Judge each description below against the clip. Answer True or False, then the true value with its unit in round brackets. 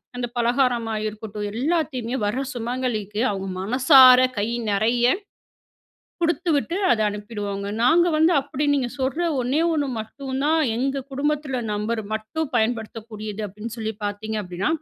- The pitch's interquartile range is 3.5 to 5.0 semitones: True (4.2 semitones)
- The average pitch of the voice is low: False (240 Hz)